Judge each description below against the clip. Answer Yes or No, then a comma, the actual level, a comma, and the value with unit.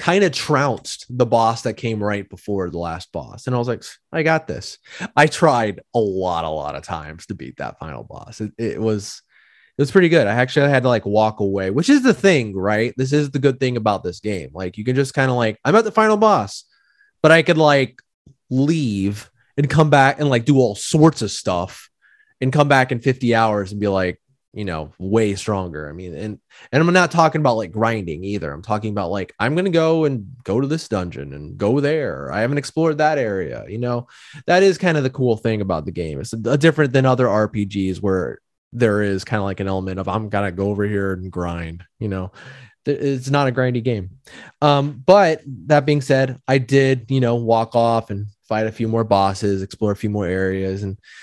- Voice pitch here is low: Yes, low, 115 Hz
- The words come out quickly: Yes, fast, 230 wpm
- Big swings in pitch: Yes, wide, 5.9 semitones